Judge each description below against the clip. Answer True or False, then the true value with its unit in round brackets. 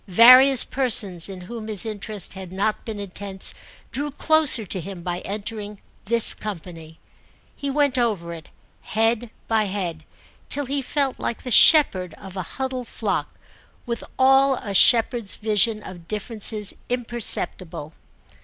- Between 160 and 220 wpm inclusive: False (140 wpm)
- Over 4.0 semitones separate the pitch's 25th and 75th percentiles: True (4.6 semitones)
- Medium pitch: False (215 Hz)